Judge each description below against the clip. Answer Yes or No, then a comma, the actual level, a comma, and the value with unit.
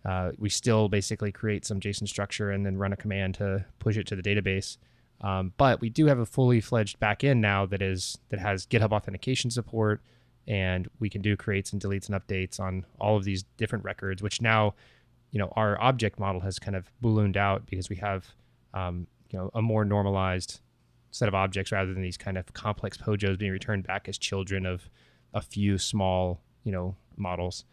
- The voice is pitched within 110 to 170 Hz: No, low, 100 Hz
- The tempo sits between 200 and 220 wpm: Yes, fast, 205 wpm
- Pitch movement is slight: Yes, narrow, 2.3 semitones